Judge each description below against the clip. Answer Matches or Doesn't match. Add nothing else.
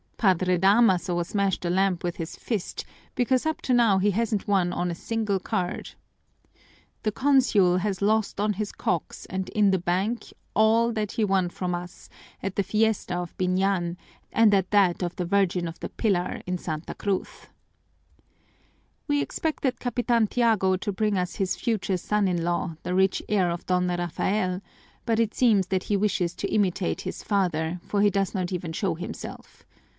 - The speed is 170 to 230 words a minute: Matches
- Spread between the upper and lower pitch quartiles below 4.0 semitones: Matches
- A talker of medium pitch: Doesn't match